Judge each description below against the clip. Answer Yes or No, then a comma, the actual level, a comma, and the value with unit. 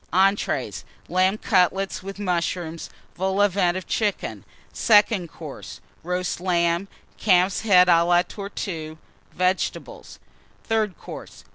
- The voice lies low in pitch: No, medium, 185 Hz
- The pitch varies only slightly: Yes, narrow, 2.1 semitones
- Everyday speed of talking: No, slow, 115 wpm